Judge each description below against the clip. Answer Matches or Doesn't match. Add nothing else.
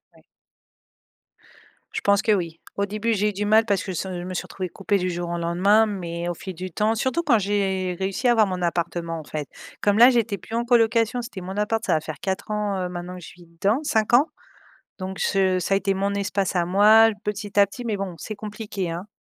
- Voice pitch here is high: Matches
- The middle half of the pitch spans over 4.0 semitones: Doesn't match